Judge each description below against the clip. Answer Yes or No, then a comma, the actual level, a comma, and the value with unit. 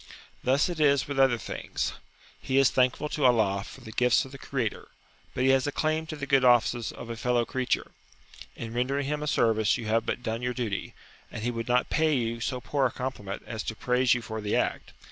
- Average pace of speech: No, fast, 230 wpm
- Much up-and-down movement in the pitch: No, average, 2.9 semitones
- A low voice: Yes, low, 125 Hz